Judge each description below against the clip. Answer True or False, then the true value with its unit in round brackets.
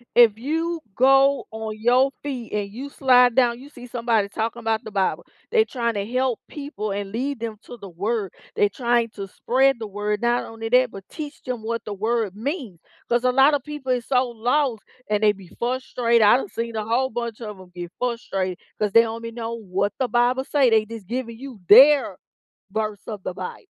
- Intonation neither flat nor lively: True (3.2 semitones)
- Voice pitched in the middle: False (235 Hz)